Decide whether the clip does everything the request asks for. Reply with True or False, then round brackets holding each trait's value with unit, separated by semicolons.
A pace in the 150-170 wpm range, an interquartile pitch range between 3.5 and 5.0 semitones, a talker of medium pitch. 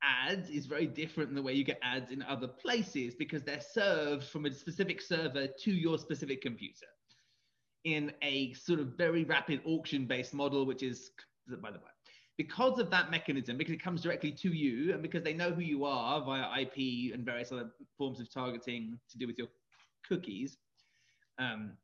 False (185 wpm; 4.1 semitones; 145 Hz)